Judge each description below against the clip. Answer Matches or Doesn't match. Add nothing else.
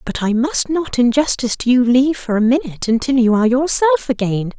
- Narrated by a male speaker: Doesn't match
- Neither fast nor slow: Doesn't match